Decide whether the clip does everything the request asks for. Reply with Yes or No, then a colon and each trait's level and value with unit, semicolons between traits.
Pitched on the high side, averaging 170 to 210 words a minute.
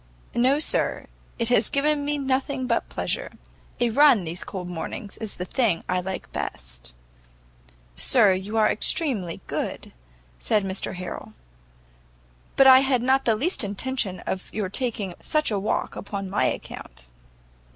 No: high, 215 Hz; average, 150 wpm